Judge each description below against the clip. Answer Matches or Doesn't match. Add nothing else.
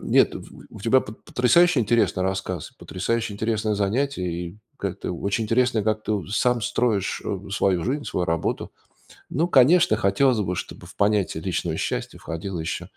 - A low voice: Matches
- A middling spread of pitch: Matches